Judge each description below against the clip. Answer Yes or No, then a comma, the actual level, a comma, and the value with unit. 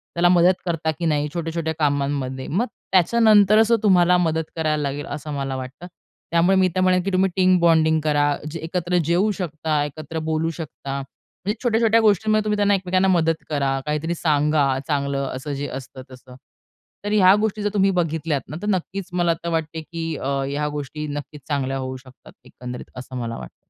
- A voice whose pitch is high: No, medium, 160 Hz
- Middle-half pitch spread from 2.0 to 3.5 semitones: No, average, 4.2 semitones